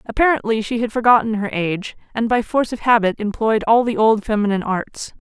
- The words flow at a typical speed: Yes, average, 195 wpm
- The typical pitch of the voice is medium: No, high, 225 Hz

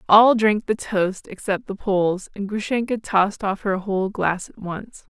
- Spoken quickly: No, average, 185 wpm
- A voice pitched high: Yes, high, 205 Hz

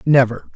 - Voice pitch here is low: Yes, low, 115 Hz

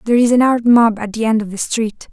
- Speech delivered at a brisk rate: Yes, fast, 310 wpm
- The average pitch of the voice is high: Yes, high, 225 Hz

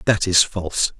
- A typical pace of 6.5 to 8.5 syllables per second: No, 4.8 syllables/s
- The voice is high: No, very low, 90 Hz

